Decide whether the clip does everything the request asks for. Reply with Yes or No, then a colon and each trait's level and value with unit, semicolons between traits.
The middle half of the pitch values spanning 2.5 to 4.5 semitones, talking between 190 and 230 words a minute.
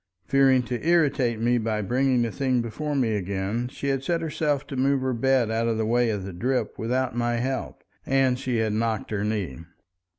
Yes: average, 3.1 semitones; fast, 205 wpm